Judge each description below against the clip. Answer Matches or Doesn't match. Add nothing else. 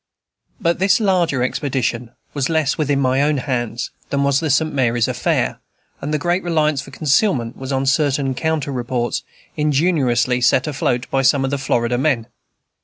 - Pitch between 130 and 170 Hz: Matches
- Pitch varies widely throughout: Doesn't match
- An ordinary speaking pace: Matches